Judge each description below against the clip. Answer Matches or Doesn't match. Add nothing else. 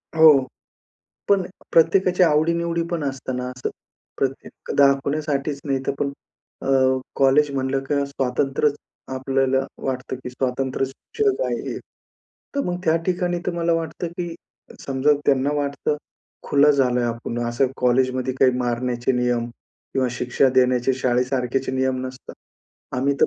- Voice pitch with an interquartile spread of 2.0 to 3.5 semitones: Matches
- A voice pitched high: Doesn't match